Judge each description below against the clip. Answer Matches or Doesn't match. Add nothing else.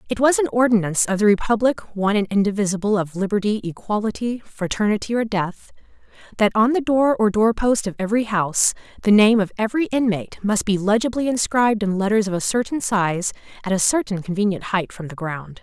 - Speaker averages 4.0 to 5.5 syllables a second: Doesn't match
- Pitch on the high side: Matches